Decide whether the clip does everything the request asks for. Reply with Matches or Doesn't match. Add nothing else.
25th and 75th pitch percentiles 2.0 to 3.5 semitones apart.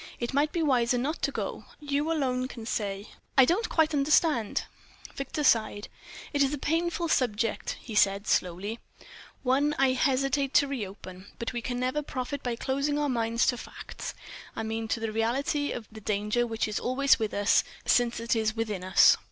Doesn't match